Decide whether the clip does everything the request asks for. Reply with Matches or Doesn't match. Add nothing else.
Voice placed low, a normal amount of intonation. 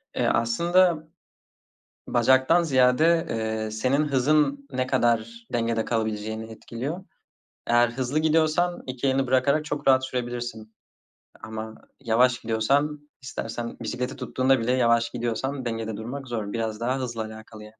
Matches